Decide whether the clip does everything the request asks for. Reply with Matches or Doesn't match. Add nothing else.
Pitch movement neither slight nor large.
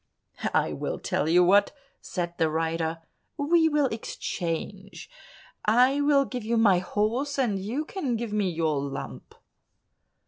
Doesn't match